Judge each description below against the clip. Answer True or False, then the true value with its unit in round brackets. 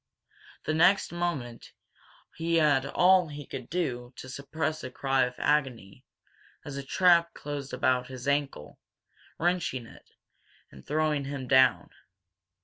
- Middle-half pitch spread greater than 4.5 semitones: False (3.7 semitones)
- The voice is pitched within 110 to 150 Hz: True (140 Hz)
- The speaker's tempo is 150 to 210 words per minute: False (135 wpm)